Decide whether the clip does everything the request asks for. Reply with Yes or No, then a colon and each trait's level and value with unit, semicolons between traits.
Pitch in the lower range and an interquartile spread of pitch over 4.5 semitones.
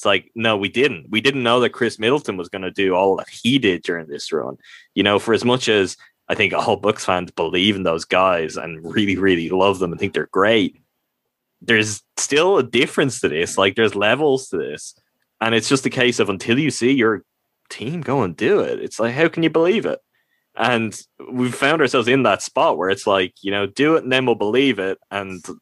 Yes: low, 110 Hz; average, 5.2 semitones